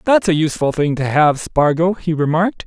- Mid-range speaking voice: Yes, medium, 160 Hz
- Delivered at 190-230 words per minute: Yes, average, 200 wpm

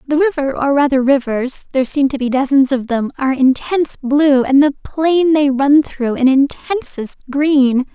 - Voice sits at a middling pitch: No, very high, 275 Hz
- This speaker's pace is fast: No, average, 165 wpm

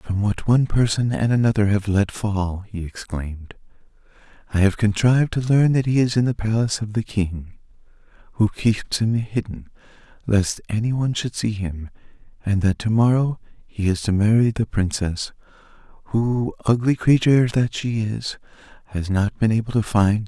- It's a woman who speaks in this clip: No, male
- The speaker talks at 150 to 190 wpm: Yes, average, 180 wpm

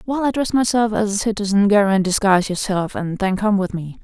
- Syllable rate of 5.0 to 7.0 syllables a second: Yes, 5.9 syllables/s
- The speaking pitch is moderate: No, high, 205 Hz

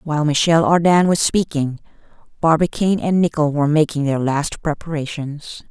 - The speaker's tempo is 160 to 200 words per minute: No, slow, 135 wpm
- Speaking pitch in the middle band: Yes, medium, 155 Hz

